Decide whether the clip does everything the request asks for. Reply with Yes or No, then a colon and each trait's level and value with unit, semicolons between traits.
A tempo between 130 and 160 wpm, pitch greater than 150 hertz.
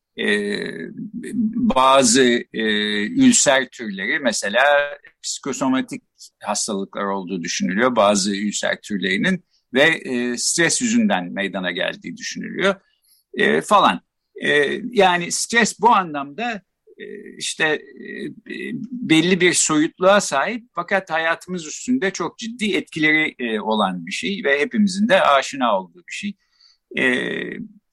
No: average, 115 wpm; high, 190 Hz